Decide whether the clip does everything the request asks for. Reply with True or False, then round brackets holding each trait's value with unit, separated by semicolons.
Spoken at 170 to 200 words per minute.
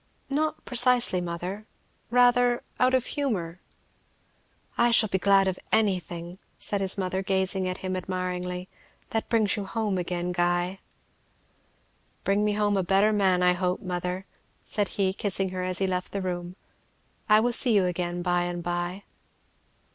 False (155 wpm)